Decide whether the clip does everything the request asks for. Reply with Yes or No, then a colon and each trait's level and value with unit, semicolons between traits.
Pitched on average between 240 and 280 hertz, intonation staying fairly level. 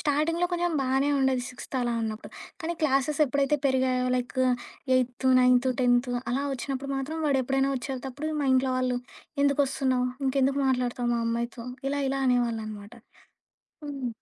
Yes: very high, 260 Hz; narrow, 2.0 semitones